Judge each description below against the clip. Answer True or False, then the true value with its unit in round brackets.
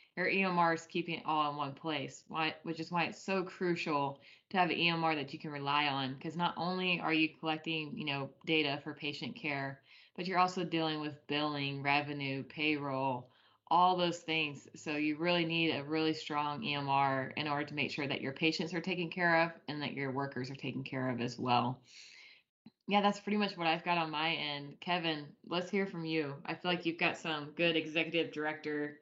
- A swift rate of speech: True (210 wpm)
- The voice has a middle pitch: True (155 Hz)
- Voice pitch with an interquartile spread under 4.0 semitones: True (3.0 semitones)